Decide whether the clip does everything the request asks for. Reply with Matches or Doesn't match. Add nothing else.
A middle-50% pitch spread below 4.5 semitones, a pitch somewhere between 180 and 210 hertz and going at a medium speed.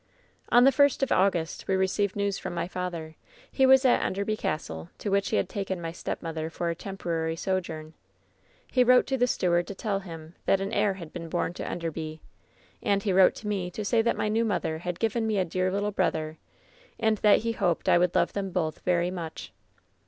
Doesn't match